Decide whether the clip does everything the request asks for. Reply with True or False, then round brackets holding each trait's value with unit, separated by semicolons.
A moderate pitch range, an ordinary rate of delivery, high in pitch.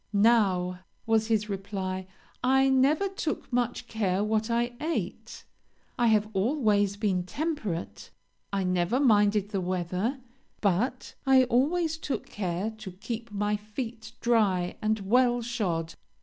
False (4.0 semitones; 130 wpm; 215 Hz)